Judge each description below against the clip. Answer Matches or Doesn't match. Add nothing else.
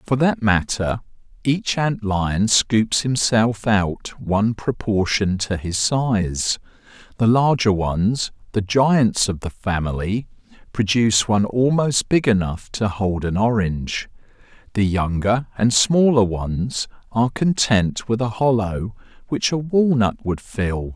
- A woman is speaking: Doesn't match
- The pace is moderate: Doesn't match